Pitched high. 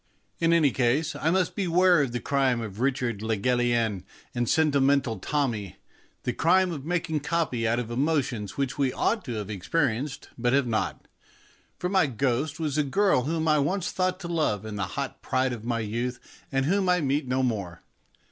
No: low, 135 Hz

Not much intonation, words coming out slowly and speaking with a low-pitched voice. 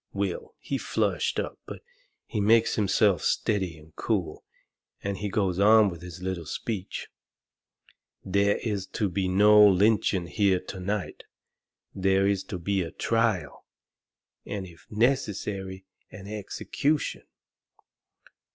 Yes: narrow, 2.2 semitones; slow, 125 wpm; low, 100 Hz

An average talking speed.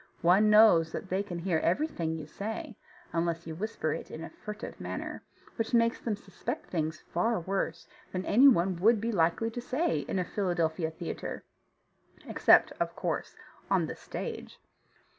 Yes: average, 165 wpm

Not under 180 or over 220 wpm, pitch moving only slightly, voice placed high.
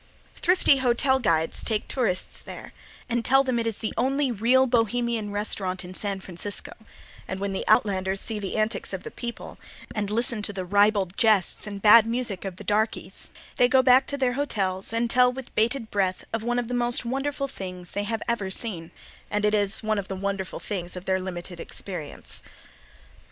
No: average, 195 wpm; average, 4.0 semitones; high, 215 Hz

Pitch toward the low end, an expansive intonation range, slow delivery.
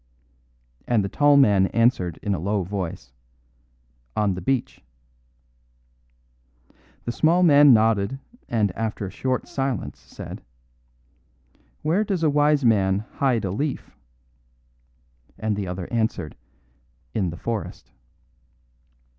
Yes: low, 110 Hz; wide, 5.9 semitones; slow, 115 wpm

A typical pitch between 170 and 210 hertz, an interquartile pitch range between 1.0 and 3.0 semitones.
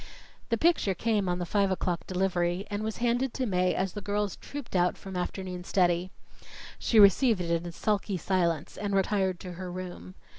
Yes: high, 190 Hz; narrow, 2.6 semitones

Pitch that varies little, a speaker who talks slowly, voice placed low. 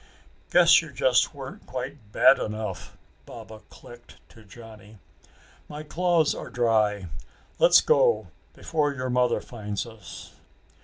No: wide, 5.4 semitones; slow, 120 wpm; low, 125 Hz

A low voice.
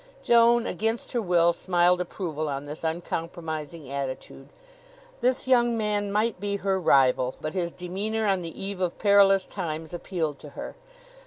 No: medium, 180 Hz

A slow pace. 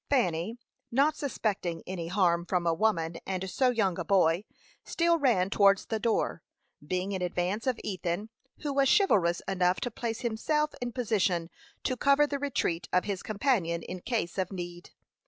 No: average, 170 wpm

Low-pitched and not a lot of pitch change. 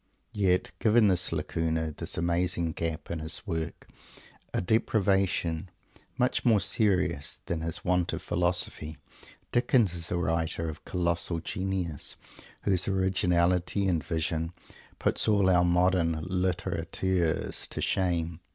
Yes: very low, 90 Hz; narrow, 2.3 semitones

